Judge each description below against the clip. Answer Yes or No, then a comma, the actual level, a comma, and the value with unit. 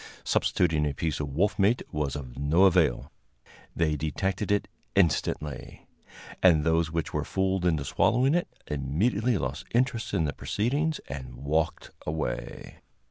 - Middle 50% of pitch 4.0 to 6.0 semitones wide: Yes, average, 5.3 semitones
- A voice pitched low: Yes, very low, 80 Hz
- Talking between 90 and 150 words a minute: Yes, average, 140 wpm